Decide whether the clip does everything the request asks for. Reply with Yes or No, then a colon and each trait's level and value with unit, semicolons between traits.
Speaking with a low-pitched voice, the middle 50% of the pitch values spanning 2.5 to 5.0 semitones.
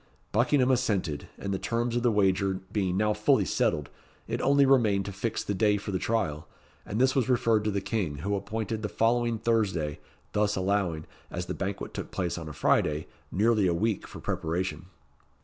Yes: low, 105 Hz; average, 3.6 semitones